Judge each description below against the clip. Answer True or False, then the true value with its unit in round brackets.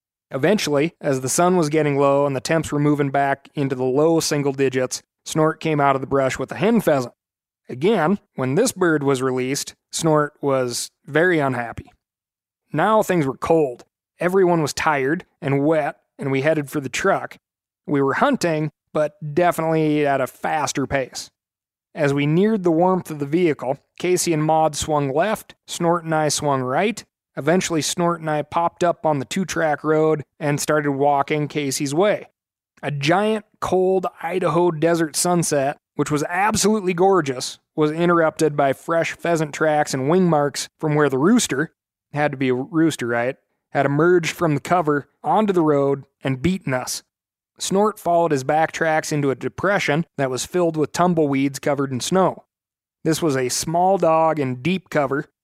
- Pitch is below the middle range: False (155 Hz)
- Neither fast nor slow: True (175 wpm)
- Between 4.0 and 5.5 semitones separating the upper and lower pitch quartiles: False (3.5 semitones)